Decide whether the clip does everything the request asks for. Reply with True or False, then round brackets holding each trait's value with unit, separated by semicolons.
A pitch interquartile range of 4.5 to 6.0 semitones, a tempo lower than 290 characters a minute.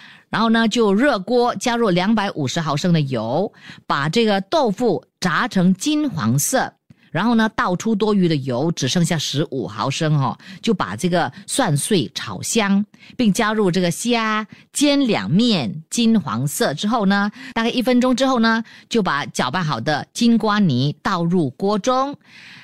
True (5.3 semitones; 235 characters per minute)